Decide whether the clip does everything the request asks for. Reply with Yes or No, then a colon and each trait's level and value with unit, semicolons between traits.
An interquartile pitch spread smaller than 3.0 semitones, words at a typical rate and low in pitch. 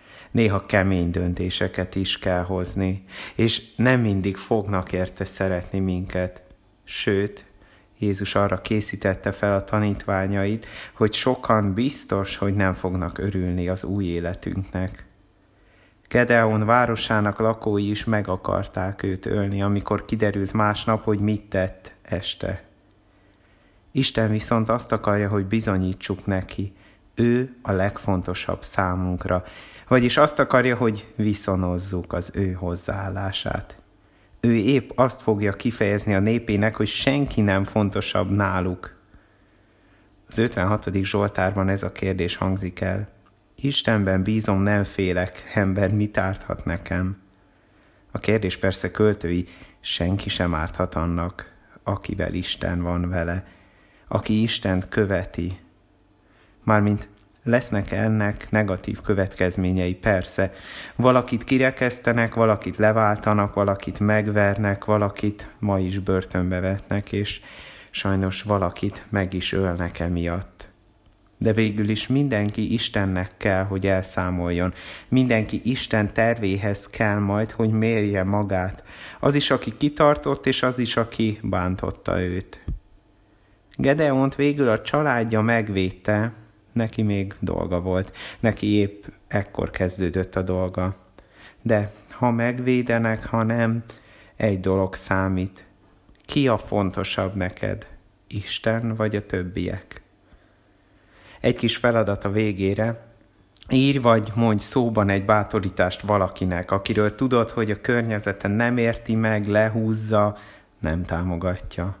Yes: narrow, 2.5 semitones; average, 115 wpm; low, 100 Hz